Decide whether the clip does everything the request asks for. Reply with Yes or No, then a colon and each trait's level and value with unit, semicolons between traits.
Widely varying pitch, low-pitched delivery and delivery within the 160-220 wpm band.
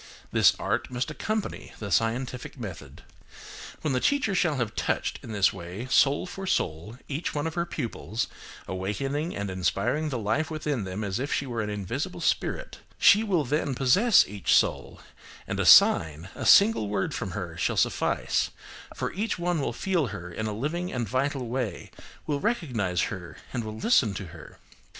Yes: wide, 7.4 semitones; low, 125 Hz; average, 180 wpm